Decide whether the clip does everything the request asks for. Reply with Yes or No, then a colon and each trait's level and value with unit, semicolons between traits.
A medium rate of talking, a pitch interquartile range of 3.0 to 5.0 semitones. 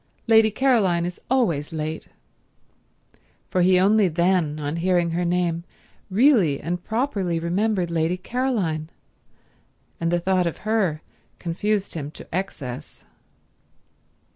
No: slow, 115 wpm; average, 3.8 semitones